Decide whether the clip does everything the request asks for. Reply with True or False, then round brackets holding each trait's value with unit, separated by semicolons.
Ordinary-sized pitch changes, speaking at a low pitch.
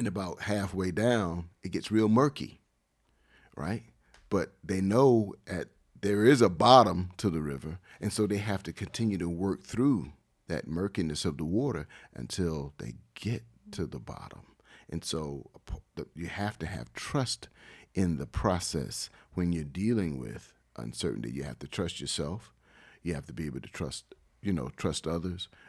True (3.9 semitones; 95 Hz)